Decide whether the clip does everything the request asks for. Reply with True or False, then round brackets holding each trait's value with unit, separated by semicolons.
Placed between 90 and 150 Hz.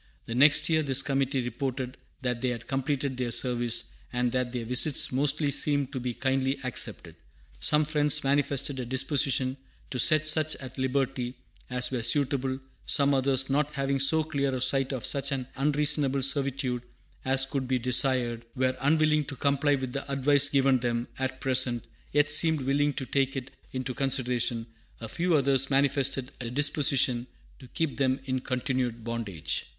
True (135 Hz)